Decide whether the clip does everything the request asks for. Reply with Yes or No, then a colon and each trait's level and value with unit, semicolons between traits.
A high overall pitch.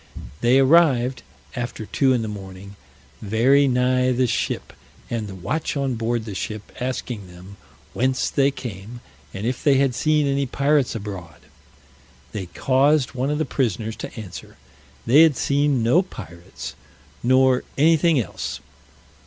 No: low, 125 Hz